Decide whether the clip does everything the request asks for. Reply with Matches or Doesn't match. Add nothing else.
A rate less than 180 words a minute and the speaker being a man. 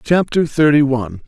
Matches